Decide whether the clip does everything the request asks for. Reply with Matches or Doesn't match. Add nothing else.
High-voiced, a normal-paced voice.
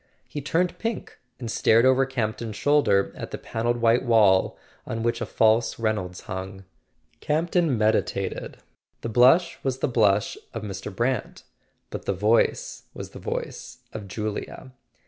Doesn't match